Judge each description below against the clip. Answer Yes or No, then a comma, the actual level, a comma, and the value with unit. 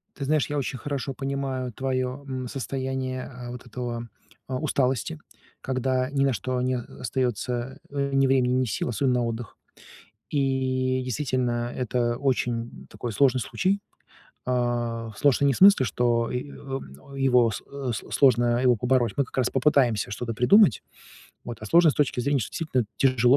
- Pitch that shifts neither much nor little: No, narrow, 2.0 semitones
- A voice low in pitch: Yes, low, 130 Hz